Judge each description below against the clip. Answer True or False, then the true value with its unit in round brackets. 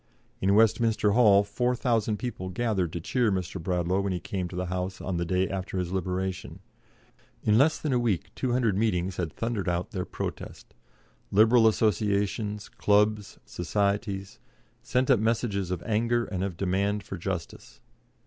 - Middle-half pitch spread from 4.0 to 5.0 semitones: False (3.3 semitones)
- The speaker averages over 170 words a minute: False (160 wpm)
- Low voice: True (100 Hz)